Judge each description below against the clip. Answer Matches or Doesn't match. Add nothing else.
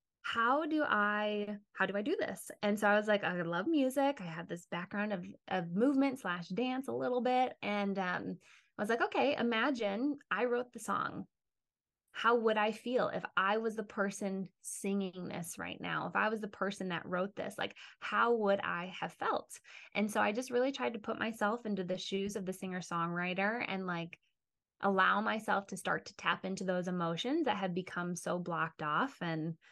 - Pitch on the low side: Doesn't match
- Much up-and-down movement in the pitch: Doesn't match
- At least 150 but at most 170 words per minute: Doesn't match